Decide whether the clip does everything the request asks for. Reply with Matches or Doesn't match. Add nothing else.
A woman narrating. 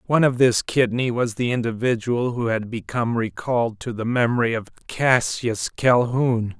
Doesn't match